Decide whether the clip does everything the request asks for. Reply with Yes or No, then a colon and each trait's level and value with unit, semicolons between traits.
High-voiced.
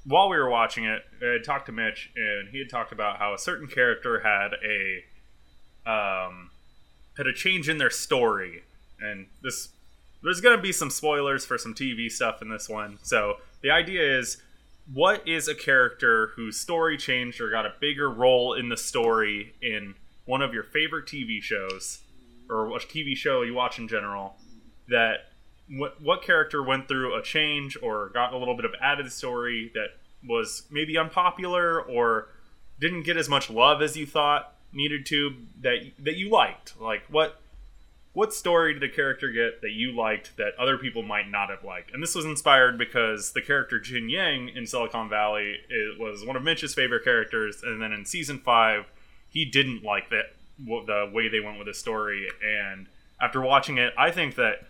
No: low, 125 Hz